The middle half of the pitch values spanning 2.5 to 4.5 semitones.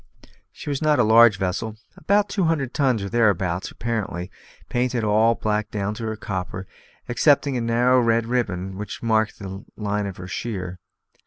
Yes: average, 3.6 semitones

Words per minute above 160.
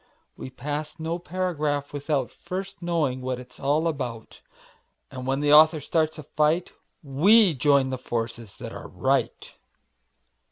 No: average, 145 wpm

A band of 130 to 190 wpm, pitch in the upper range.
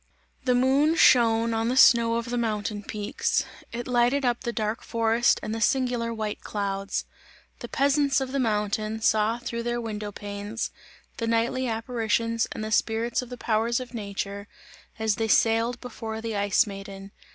Yes: average, 170 wpm; high, 230 Hz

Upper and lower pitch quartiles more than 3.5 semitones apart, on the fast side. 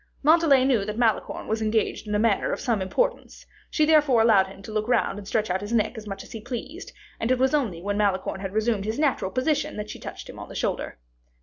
Yes: average, 4.2 semitones; fast, 240 wpm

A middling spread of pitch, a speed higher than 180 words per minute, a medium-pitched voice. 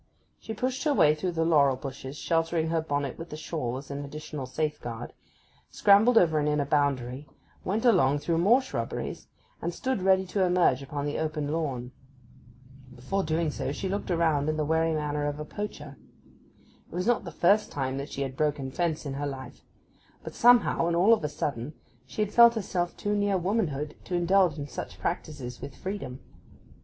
Yes: average, 4.6 semitones; average, 190 wpm; medium, 155 Hz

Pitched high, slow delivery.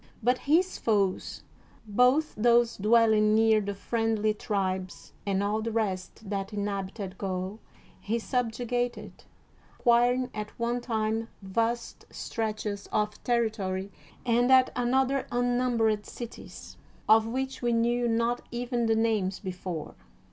Yes: high, 225 Hz; slow, 125 wpm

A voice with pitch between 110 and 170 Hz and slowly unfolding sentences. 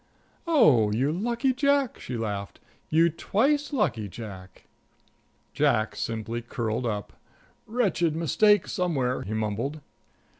Yes: medium, 140 Hz; slow, 110 wpm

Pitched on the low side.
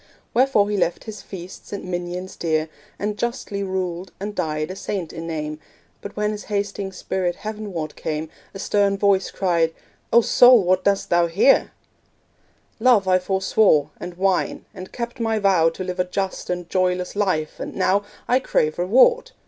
No: high, 190 Hz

